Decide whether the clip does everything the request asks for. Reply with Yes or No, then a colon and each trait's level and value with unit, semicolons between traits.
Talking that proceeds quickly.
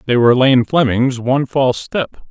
No: average, 180 wpm